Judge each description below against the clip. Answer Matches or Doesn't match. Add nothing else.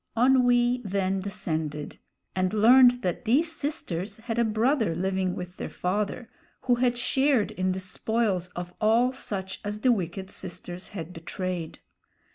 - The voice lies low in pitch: Doesn't match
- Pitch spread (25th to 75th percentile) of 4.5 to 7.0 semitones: Matches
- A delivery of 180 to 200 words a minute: Doesn't match